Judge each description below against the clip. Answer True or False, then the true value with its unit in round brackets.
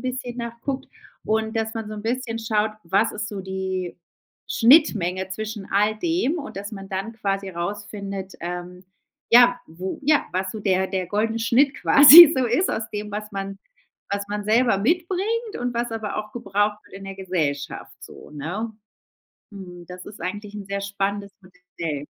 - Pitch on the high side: True (205 Hz)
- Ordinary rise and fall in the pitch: True (3.3 semitones)